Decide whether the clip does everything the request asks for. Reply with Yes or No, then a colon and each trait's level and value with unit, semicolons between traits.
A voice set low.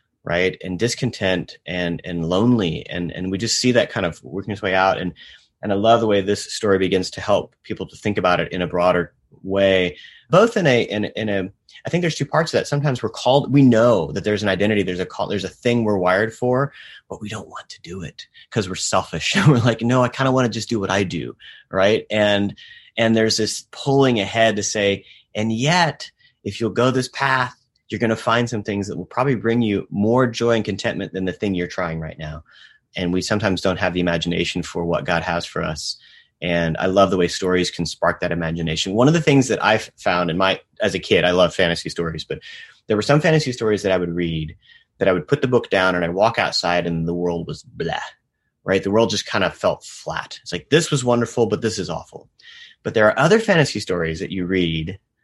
Yes: low, 100 Hz